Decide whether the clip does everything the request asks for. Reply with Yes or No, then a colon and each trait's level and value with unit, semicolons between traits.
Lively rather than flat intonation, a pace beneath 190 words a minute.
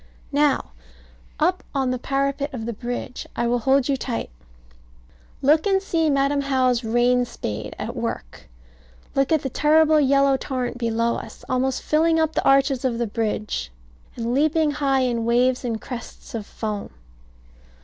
No: average, 3.2 semitones; average, 160 wpm